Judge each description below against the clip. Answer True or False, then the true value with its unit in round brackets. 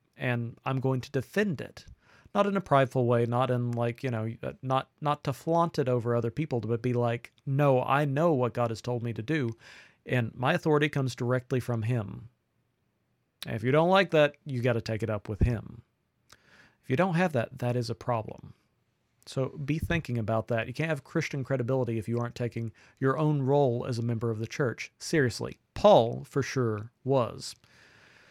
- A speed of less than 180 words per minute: False (200 wpm)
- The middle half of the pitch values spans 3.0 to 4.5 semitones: True (3.3 semitones)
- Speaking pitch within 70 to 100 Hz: False (125 Hz)